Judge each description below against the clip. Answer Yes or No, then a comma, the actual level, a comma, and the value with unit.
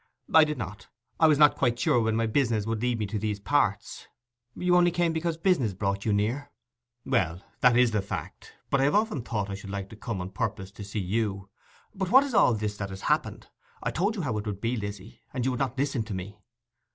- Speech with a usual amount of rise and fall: No, wide, 5.9 semitones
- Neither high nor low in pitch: No, low, 115 Hz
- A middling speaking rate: No, fast, 235 wpm